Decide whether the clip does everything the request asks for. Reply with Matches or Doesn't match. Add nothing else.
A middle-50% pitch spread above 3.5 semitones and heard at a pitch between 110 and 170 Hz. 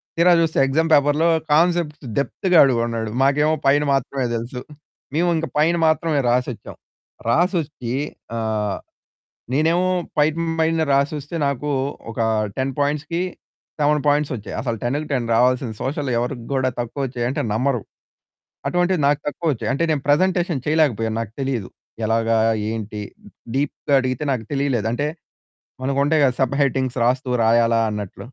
Matches